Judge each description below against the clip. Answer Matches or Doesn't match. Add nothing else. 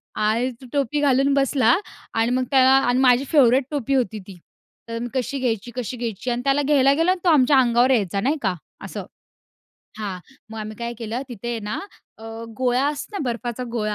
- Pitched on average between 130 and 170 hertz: Doesn't match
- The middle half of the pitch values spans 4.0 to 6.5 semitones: Doesn't match